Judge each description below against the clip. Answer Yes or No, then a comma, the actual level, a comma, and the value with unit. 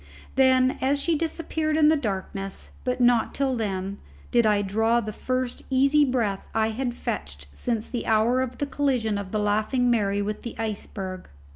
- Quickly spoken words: No, average, 175 wpm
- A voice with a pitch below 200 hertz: No, high, 235 Hz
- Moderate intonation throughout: Yes, average, 4.0 semitones